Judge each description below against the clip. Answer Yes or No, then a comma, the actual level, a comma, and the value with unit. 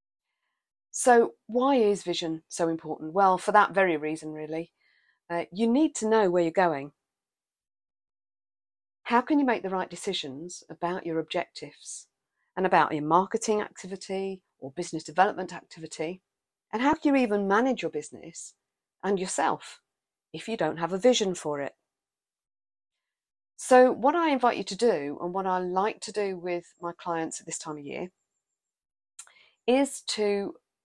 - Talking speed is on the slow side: No, average, 155 wpm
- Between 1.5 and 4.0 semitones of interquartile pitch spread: No, average, 5.0 semitones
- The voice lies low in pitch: No, medium, 185 Hz